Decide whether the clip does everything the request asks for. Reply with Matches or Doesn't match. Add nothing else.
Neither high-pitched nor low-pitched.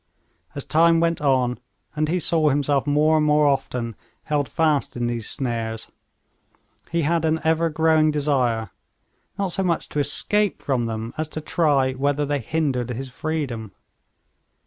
Matches